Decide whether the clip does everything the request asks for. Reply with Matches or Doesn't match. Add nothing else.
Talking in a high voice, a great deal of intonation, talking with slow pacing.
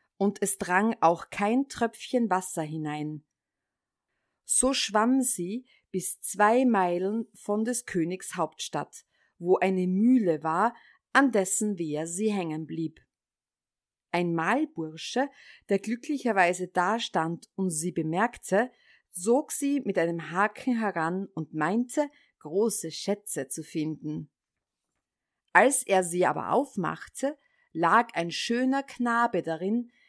Matches